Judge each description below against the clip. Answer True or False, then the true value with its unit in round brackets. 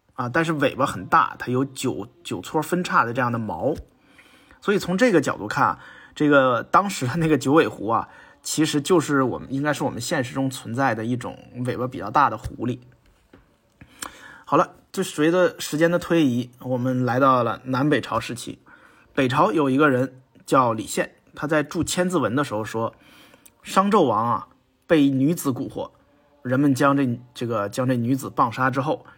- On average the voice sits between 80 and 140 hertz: True (135 Hz)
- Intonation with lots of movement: False (3.8 semitones)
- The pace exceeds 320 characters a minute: False (260 characters per minute)